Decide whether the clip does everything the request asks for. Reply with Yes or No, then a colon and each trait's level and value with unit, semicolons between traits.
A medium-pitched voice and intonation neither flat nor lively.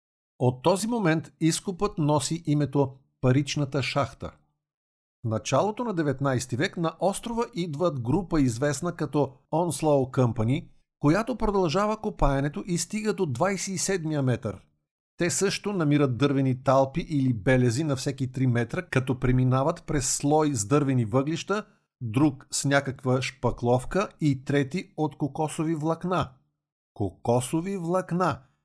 Yes: medium, 145 Hz; average, 4.7 semitones